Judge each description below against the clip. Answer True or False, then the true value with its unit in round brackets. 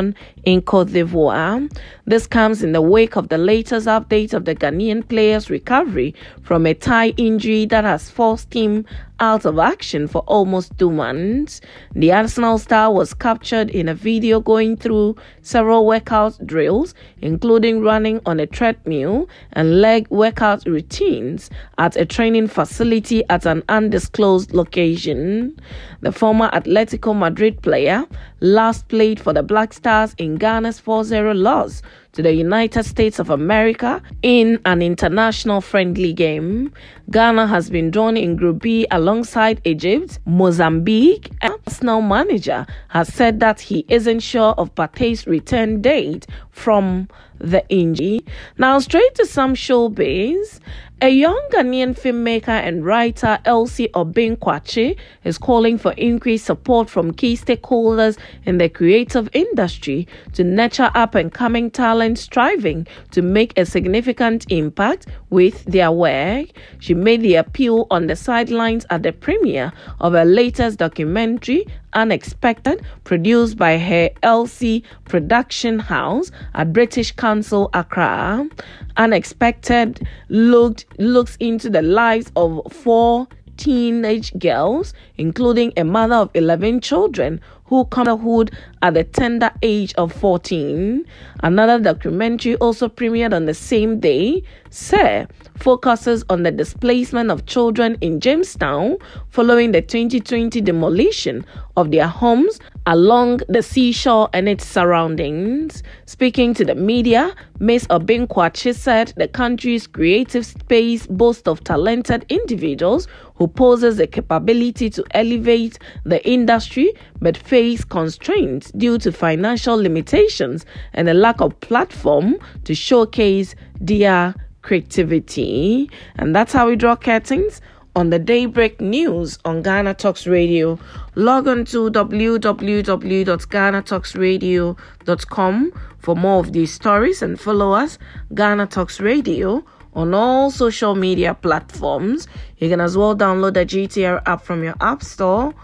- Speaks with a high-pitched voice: True (220 Hz)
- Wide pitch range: False (4.5 semitones)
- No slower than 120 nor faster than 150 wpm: True (135 wpm)